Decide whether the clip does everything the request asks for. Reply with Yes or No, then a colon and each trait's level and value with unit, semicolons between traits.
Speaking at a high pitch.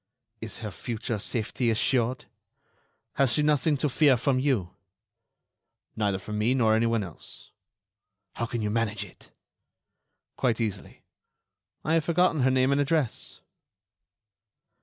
No: low, 120 Hz